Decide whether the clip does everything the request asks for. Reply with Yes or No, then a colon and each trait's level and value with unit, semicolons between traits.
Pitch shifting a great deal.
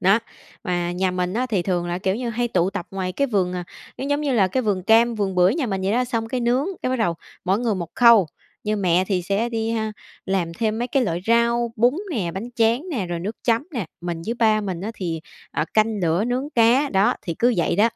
No: average, 4.5 semitones